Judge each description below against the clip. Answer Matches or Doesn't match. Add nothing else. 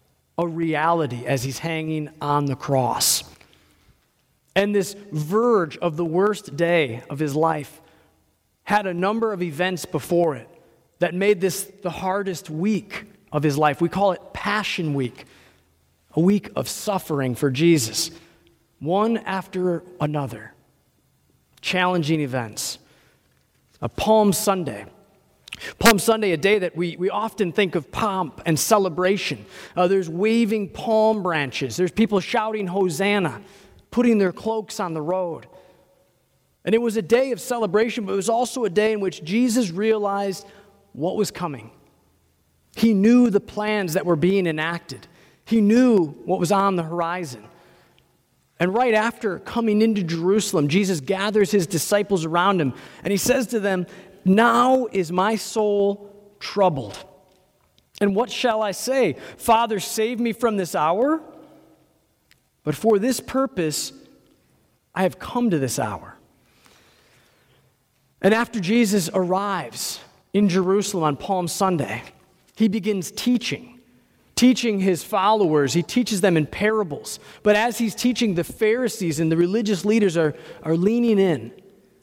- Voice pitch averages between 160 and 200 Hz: Matches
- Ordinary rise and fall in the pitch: Matches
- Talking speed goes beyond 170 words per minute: Doesn't match